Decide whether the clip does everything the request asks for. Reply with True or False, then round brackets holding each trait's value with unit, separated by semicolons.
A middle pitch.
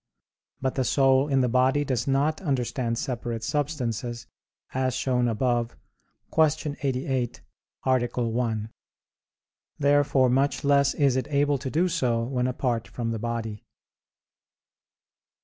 False (130 Hz)